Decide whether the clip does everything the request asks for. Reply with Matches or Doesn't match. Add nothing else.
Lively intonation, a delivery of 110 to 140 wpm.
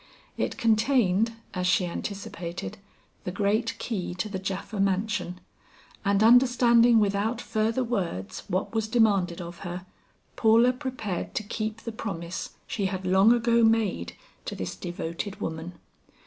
Doesn't match